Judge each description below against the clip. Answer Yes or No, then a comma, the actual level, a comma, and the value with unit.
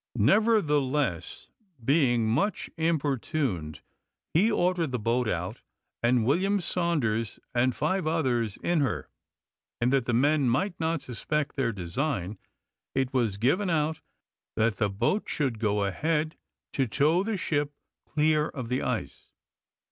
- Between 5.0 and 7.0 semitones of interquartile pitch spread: Yes, wide, 5.5 semitones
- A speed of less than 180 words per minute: Yes, slow, 135 wpm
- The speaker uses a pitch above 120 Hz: Yes, medium, 140 Hz